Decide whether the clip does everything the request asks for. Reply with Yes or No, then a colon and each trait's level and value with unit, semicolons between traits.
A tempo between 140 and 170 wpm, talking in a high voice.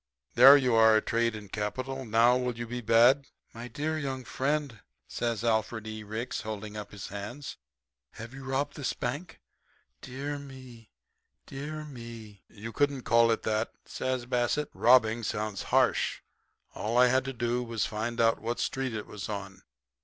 No: average, 165 wpm; low, 120 Hz